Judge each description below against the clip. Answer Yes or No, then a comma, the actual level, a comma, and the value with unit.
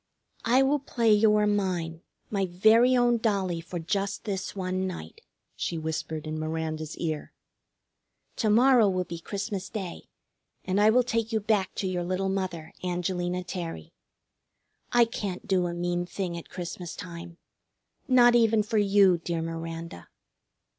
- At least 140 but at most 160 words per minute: Yes, average, 155 wpm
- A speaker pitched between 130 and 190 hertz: Yes, medium, 185 Hz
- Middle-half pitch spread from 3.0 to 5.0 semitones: Yes, average, 3.9 semitones